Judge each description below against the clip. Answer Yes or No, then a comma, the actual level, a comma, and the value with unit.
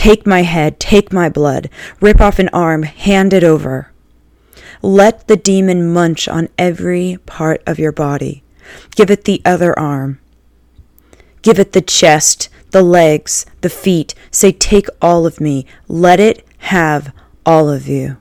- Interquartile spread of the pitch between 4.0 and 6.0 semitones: Yes, average, 4.5 semitones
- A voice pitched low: No, medium, 170 Hz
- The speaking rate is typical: Yes, average, 155 wpm